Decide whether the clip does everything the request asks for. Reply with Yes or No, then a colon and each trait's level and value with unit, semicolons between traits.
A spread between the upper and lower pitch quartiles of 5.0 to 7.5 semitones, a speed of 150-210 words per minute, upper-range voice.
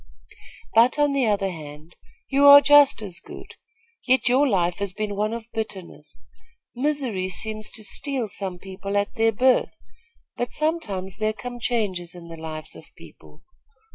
Yes: average, 5.3 semitones; average, 160 wpm; high, 215 Hz